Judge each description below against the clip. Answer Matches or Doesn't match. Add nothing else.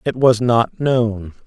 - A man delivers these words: Matches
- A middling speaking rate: Matches